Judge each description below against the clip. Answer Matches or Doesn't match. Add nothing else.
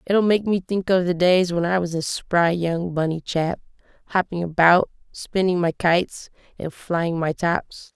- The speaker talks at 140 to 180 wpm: Doesn't match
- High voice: Doesn't match